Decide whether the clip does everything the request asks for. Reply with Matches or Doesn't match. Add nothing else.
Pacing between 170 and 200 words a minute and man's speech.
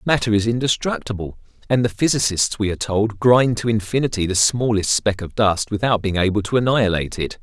Matches